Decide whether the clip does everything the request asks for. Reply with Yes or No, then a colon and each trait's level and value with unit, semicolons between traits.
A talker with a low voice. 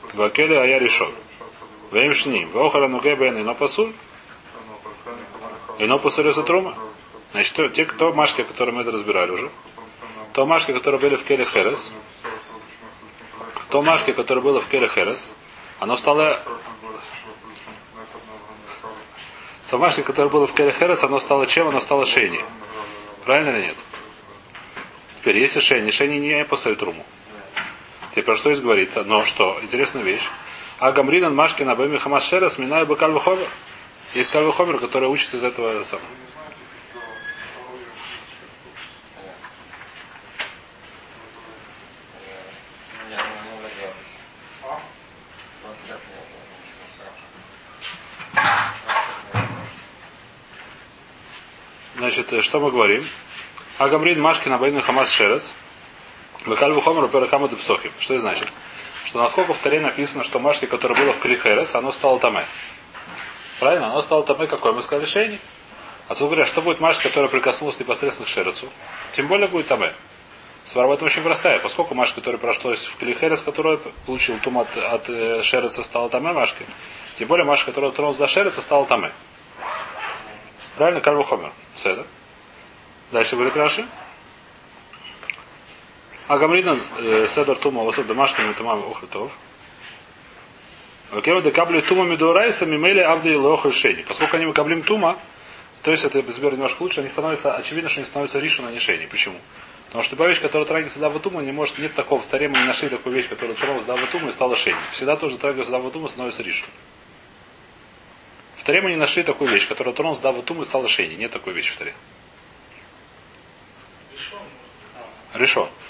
No: medium, 145 Hz